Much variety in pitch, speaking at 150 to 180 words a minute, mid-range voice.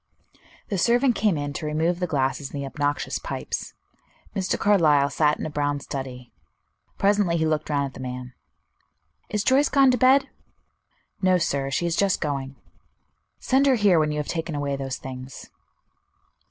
Yes: wide, 6.1 semitones; average, 170 wpm; medium, 155 Hz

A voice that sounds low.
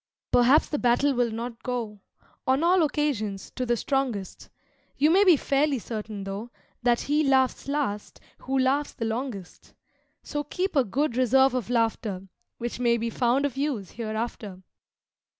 No: high, 245 Hz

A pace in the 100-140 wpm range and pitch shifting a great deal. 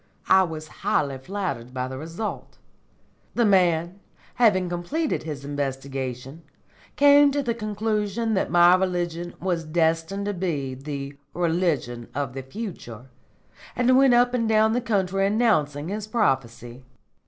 Yes: slow, 135 wpm; wide, 7.2 semitones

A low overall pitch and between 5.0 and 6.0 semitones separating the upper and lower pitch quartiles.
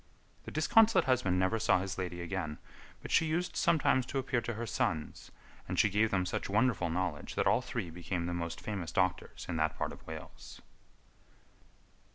Yes: very low, 95 Hz; wide, 5.5 semitones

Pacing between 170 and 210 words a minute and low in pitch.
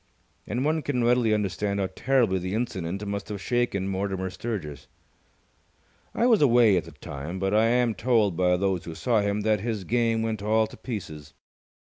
Yes: average, 180 wpm; low, 105 Hz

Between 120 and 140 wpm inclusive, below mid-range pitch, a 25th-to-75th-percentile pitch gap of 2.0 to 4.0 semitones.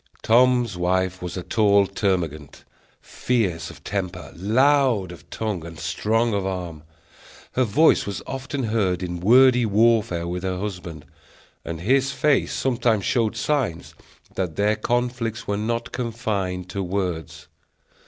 No: slow, 135 wpm; low, 100 Hz; average, 4.7 semitones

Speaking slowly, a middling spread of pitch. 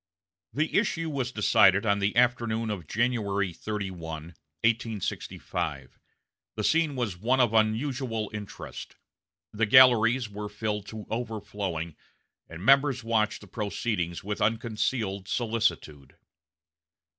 Yes: slow, 110 wpm; average, 3.1 semitones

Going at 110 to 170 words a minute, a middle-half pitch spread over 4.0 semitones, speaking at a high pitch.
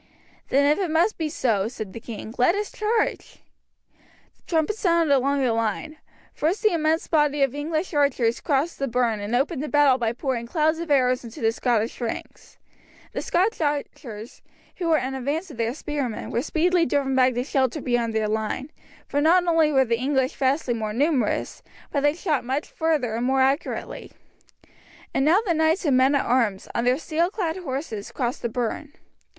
No: average, 190 wpm; average, 4.6 semitones; very high, 275 Hz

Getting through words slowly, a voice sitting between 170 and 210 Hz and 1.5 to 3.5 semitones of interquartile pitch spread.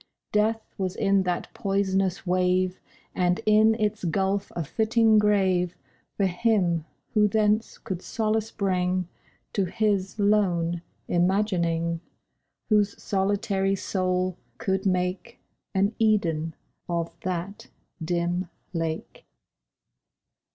Yes: slow, 100 wpm; high, 190 Hz; average, 2.8 semitones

